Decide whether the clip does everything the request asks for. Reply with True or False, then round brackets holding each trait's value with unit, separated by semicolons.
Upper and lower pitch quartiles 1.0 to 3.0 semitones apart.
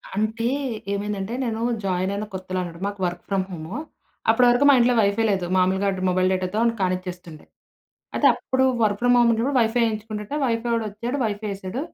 False (3.6 semitones)